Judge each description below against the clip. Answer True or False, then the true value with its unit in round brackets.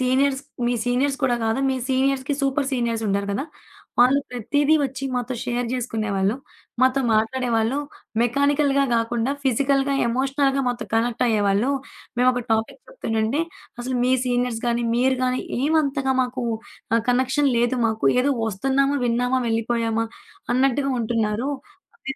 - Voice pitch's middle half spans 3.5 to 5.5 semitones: False (2.9 semitones)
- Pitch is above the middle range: True (250 Hz)